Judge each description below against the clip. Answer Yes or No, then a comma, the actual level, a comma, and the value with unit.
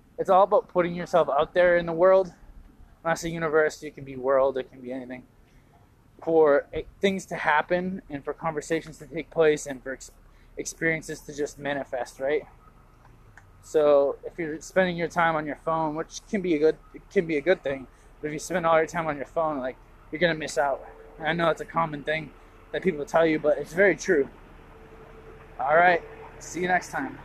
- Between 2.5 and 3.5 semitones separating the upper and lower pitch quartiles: Yes, average, 3.0 semitones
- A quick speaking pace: Yes, fast, 210 wpm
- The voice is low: No, medium, 155 Hz